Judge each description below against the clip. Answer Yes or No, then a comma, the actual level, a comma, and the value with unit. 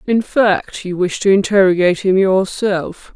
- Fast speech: No, average, 150 wpm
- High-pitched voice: Yes, high, 195 Hz